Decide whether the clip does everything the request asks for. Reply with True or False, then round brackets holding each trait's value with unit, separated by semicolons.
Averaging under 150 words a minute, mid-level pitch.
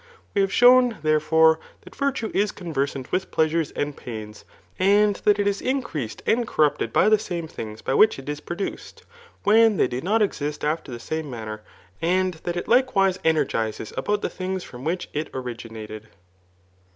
False (175 wpm; 165 Hz)